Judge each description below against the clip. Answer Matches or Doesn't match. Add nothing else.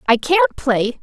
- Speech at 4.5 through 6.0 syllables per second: Doesn't match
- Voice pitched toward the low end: Doesn't match